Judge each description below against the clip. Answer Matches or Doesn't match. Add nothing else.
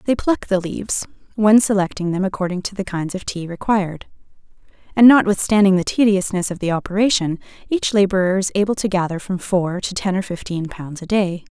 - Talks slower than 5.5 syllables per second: Doesn't match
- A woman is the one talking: Matches